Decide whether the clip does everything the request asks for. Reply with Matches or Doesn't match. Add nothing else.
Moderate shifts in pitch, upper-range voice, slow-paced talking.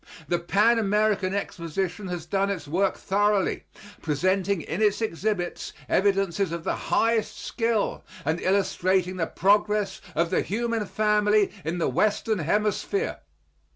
Matches